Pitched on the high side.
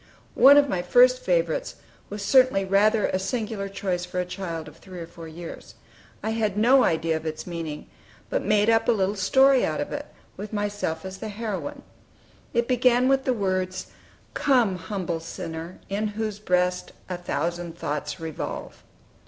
Yes: high, 195 Hz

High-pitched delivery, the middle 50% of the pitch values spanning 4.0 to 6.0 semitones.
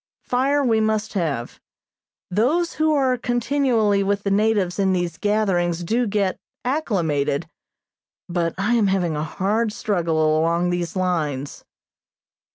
Yes: high, 200 Hz; average, 4.8 semitones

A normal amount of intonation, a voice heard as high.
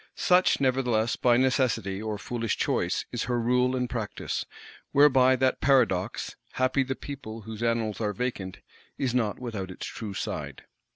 No: average, 3.0 semitones; low, 120 Hz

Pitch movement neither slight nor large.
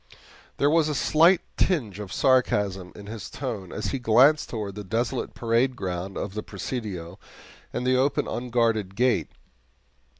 Yes: average, 4.4 semitones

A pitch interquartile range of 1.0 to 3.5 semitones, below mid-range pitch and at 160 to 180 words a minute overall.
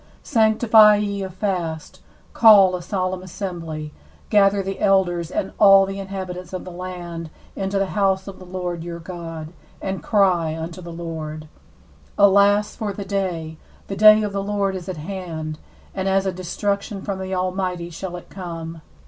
No: narrow, 2.4 semitones; medium, 185 Hz; average, 170 wpm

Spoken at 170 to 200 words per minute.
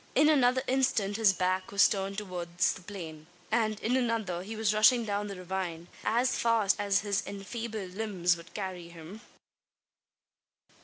No: average, 155 wpm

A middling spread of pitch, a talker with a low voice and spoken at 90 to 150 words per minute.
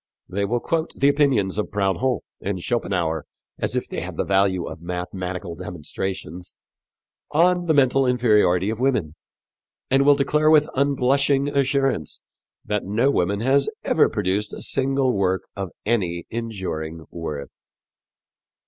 No: wide, 6.9 semitones; low, 105 Hz; average, 145 wpm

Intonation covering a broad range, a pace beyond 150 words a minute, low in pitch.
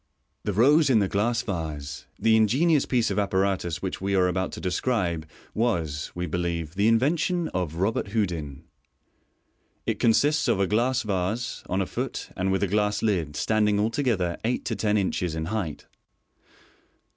No: average, 4.4 semitones; average, 170 wpm; low, 100 Hz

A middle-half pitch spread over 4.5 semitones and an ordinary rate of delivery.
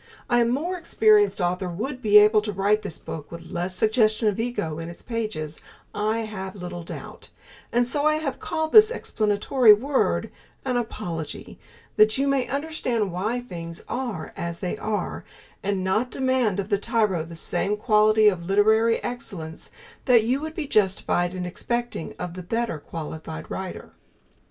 Yes: average, 5.3 semitones; average, 165 wpm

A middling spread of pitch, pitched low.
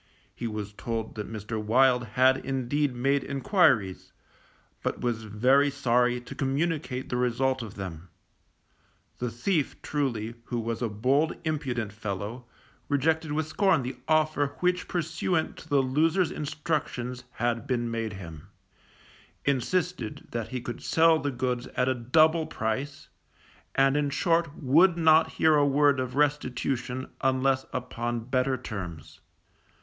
Yes: average, 4.0 semitones; low, 130 Hz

